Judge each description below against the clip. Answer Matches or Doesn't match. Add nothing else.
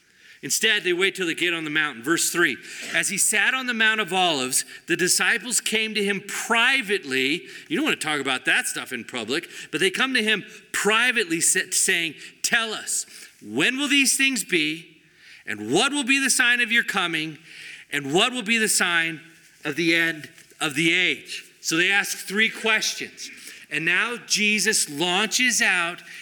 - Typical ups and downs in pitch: Doesn't match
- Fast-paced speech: Doesn't match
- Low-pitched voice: Doesn't match